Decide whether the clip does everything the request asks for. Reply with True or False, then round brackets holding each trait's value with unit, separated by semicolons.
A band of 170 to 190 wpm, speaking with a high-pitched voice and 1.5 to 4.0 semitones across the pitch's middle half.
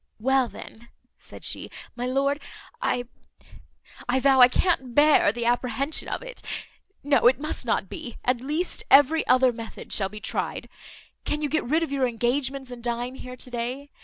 True (175 wpm; 255 Hz; 2.9 semitones)